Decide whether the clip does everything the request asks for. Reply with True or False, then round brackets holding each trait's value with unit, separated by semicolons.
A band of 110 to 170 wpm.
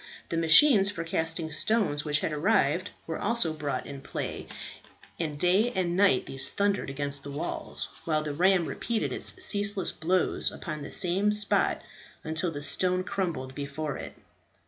True (160 wpm)